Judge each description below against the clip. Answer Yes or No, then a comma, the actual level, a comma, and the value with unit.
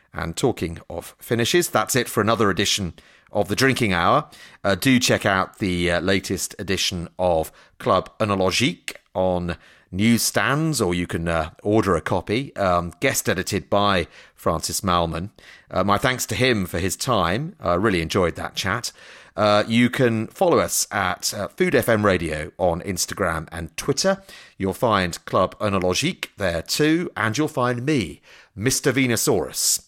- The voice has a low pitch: Yes, low, 100 Hz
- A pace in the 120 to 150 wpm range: No, average, 160 wpm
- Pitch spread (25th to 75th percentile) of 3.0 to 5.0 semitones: No, wide, 5.5 semitones